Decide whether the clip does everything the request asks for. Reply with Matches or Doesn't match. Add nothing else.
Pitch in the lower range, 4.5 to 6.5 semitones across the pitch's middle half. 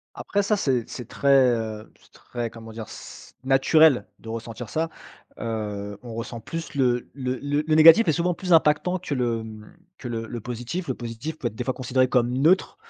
Matches